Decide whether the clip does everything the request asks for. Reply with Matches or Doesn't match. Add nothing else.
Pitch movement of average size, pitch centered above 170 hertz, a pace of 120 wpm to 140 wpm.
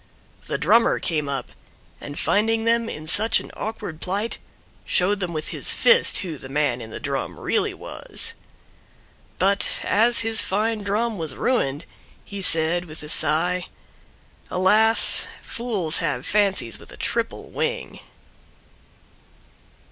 Doesn't match